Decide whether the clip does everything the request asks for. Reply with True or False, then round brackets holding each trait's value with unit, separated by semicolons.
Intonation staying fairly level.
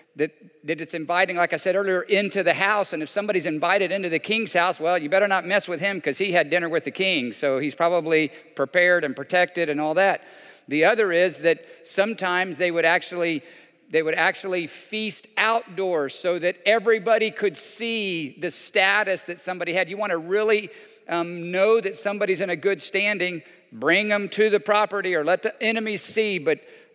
False (3.6 semitones)